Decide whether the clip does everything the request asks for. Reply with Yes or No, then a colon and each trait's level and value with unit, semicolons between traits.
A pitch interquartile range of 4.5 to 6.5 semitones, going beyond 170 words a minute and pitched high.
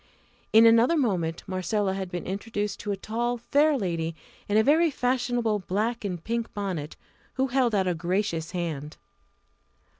No: average, 4.8 semitones; average, 155 wpm; high, 205 Hz